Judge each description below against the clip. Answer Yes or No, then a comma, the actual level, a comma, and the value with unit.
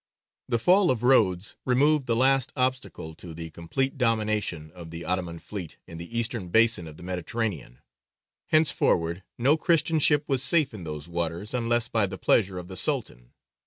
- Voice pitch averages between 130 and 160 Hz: No, low, 110 Hz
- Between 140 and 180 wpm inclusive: Yes, average, 170 wpm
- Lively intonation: Yes, wide, 7.1 semitones